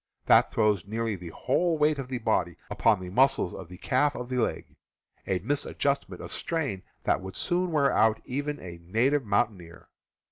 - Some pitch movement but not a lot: No, wide, 7.1 semitones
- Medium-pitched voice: No, low, 115 Hz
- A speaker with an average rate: Yes, average, 185 wpm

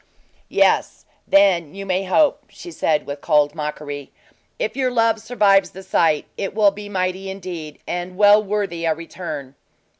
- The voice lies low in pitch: No, medium, 185 Hz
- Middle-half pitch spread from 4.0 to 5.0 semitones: Yes, average, 4.3 semitones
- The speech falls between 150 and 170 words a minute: Yes, average, 155 wpm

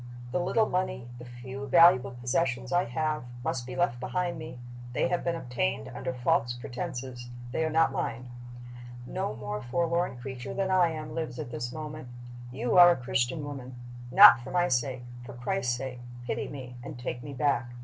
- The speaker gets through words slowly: No, average, 180 wpm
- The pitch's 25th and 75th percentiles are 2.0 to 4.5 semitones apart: No, average, 5.0 semitones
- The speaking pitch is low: Yes, low, 130 Hz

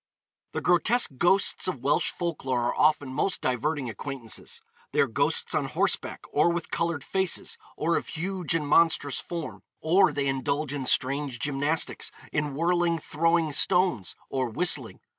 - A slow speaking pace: No, average, 155 wpm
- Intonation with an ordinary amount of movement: Yes, average, 3.9 semitones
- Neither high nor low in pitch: Yes, medium, 150 Hz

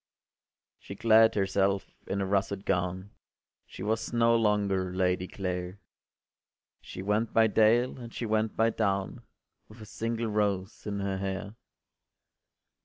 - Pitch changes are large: No, narrow, 2.6 semitones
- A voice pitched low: Yes, low, 100 Hz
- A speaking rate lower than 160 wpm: Yes, average, 140 wpm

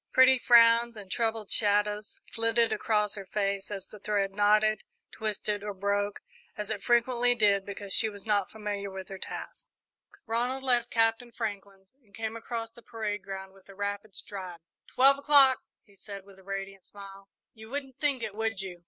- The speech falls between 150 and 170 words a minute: No, average, 180 wpm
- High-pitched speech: Yes, high, 210 Hz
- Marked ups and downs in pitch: No, narrow, 2.6 semitones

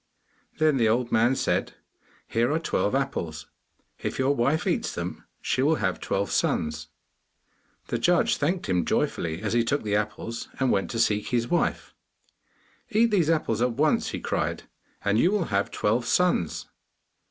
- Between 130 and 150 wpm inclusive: No, average, 165 wpm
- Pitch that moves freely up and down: Yes, wide, 6.1 semitones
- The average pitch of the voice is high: No, low, 120 Hz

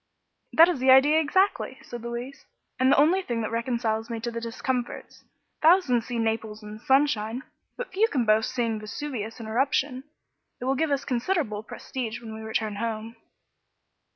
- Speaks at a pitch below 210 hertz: No, high, 240 Hz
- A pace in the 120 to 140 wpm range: No, average, 170 wpm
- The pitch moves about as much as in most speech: Yes, average, 4.0 semitones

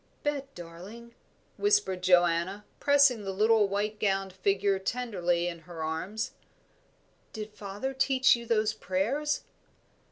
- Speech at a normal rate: No, slow, 120 wpm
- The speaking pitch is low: No, high, 205 Hz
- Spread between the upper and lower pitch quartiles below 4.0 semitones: No, average, 4.3 semitones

